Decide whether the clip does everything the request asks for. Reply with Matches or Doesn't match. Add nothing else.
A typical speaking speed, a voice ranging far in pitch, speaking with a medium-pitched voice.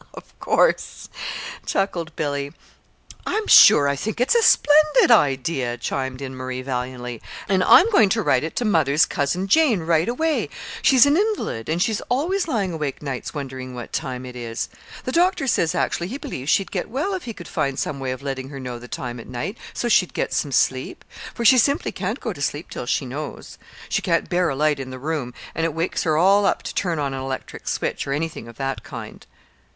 Doesn't match